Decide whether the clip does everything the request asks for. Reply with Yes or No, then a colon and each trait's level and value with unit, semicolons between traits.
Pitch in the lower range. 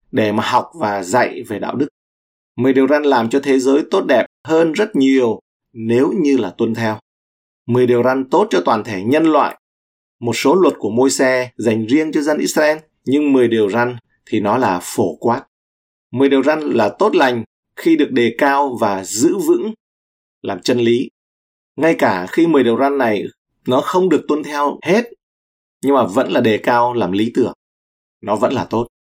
Yes: low, 125 Hz